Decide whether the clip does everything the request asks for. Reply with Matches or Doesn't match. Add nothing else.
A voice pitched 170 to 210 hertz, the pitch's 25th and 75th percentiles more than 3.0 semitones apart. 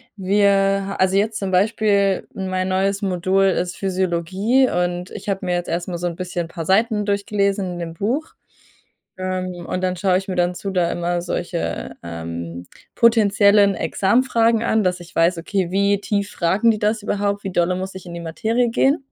Doesn't match